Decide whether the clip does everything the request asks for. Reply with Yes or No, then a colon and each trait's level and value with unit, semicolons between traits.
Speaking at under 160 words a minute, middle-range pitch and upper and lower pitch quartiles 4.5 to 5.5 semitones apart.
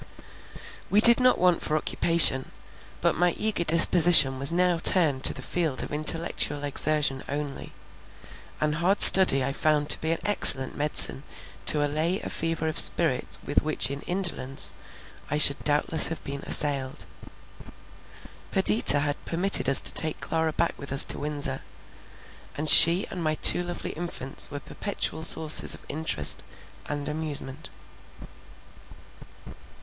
No: average, 145 wpm; medium, 155 Hz; average, 3.0 semitones